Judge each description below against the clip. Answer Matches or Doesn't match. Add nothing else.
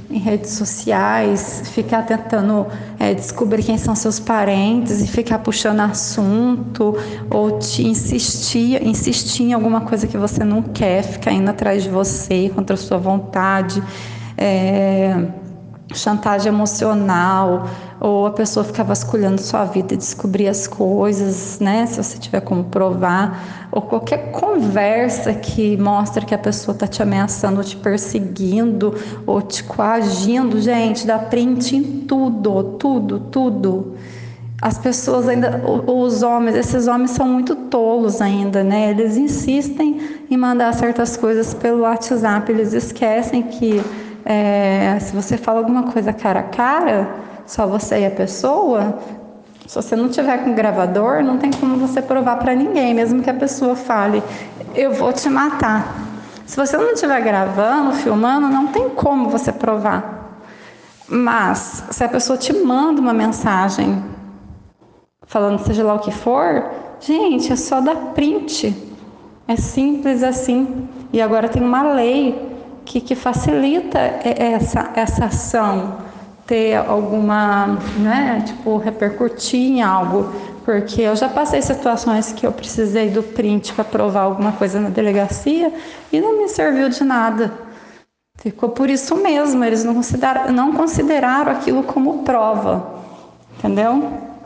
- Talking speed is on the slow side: Doesn't match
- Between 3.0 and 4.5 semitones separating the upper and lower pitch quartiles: Matches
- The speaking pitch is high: Matches